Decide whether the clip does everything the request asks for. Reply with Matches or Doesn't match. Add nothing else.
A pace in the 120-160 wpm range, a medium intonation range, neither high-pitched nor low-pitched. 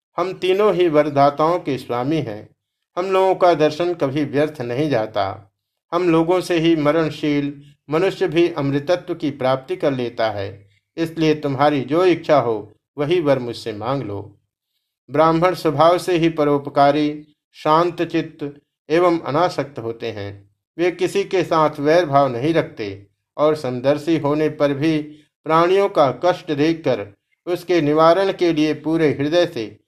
Matches